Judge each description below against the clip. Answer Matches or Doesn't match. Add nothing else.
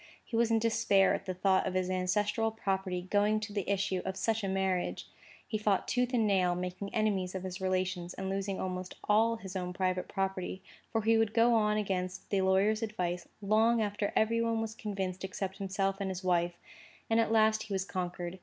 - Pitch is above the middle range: Matches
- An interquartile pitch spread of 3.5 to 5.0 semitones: Doesn't match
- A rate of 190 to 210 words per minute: Matches